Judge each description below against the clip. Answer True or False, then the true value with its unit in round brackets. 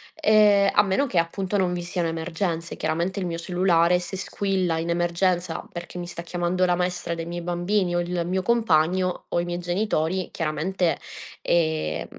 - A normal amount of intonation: False (1.7 semitones)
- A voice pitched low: False (175 Hz)